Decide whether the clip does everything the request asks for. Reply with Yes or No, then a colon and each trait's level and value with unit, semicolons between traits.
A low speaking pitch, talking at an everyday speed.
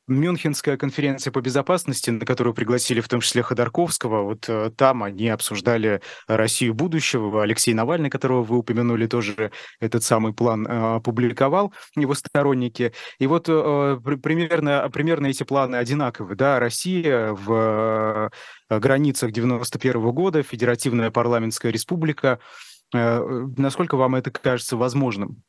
Yes: low, 125 Hz; average, 120 wpm